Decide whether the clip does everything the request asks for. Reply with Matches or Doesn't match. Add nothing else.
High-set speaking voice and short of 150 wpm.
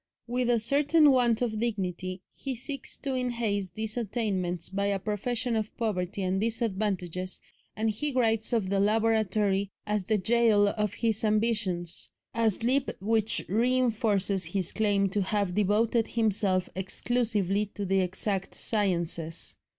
Matches